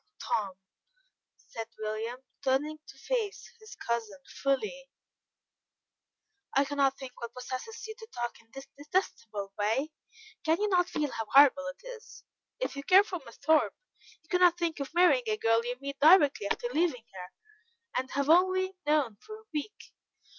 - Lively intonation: Yes, wide, 7.2 semitones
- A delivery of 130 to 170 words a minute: Yes, average, 160 wpm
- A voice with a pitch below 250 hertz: No, very high, 285 Hz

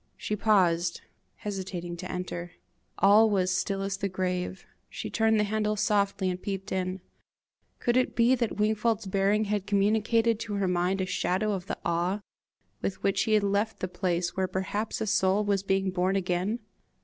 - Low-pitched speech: No, high, 195 Hz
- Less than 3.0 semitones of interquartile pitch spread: Yes, narrow, 2.4 semitones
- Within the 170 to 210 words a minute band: Yes, average, 175 wpm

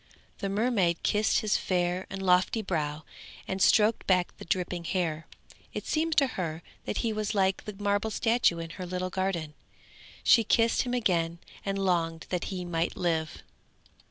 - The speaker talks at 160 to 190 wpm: Yes, average, 165 wpm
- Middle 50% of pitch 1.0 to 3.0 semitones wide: No, average, 3.7 semitones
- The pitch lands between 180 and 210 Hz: Yes, medium, 185 Hz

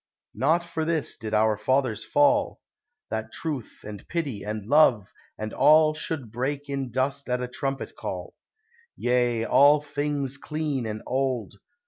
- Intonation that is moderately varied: Yes, average, 4.7 semitones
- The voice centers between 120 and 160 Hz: Yes, low, 135 Hz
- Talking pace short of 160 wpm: Yes, average, 145 wpm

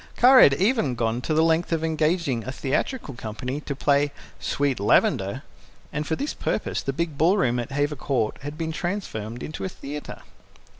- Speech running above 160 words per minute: Yes, average, 180 wpm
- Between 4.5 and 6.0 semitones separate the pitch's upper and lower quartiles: No, average, 4.0 semitones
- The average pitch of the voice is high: No, medium, 145 Hz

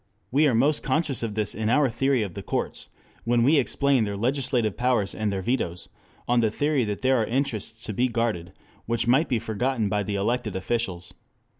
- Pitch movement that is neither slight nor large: Yes, average, 3.7 semitones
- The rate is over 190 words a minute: Yes, average, 200 wpm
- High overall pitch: No, low, 115 Hz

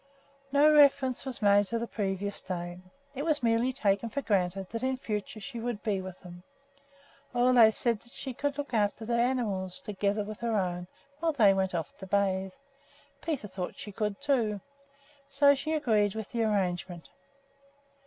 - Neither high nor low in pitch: No, high, 215 Hz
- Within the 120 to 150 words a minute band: No, average, 175 wpm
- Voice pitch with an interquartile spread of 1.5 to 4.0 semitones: No, average, 4.6 semitones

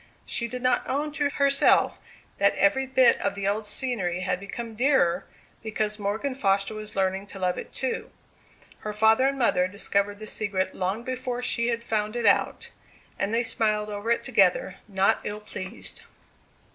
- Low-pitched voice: No, high, 215 Hz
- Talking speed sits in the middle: Yes, average, 170 wpm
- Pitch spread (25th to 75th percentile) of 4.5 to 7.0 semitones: No, average, 3.8 semitones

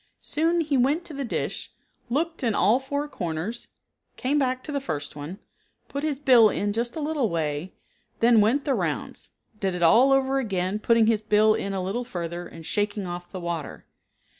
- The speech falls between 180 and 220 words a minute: Yes, average, 190 wpm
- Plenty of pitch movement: Yes, wide, 6.8 semitones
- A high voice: Yes, high, 225 Hz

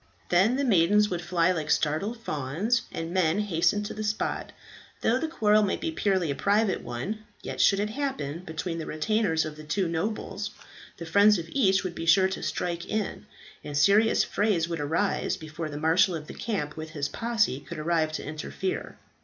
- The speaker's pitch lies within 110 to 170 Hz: No, medium, 185 Hz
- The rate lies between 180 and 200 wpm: Yes, average, 190 wpm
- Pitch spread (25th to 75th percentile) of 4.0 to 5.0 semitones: Yes, average, 4.7 semitones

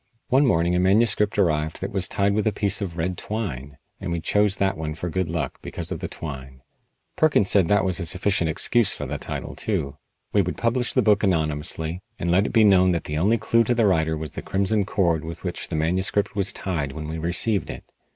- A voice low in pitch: Yes, very low, 95 Hz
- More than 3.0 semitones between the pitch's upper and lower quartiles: Yes, average, 4.2 semitones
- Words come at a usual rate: No, fast, 230 wpm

